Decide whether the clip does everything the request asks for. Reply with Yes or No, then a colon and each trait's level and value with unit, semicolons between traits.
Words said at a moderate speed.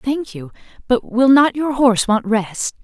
Yes: average, 190 wpm